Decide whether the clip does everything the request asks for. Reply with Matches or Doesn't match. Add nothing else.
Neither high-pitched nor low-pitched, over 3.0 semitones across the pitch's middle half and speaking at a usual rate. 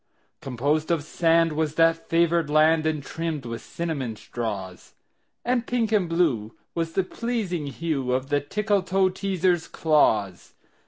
Doesn't match